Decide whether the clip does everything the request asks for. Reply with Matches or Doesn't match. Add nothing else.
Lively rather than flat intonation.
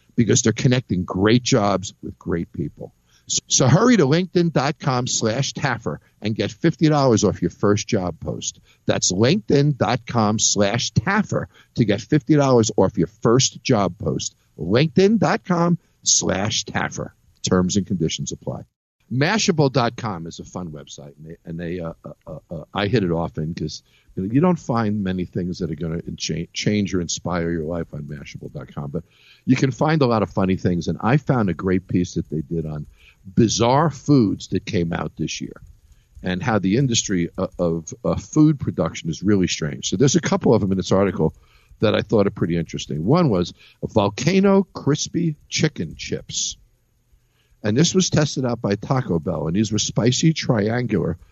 Matches